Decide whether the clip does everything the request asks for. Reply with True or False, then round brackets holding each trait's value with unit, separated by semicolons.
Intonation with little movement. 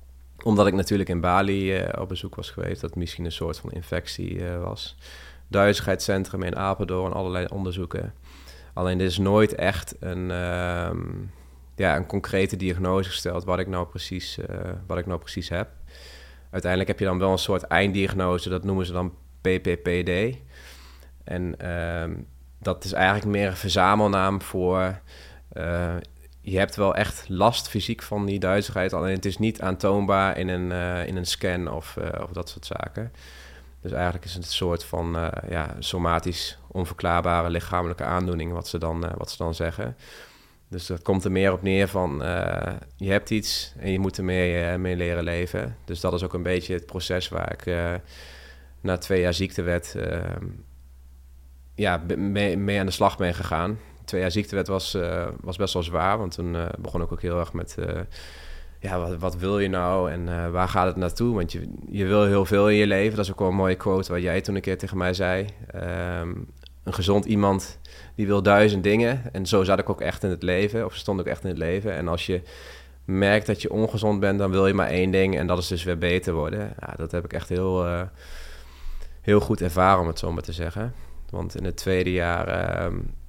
True (2.3 semitones)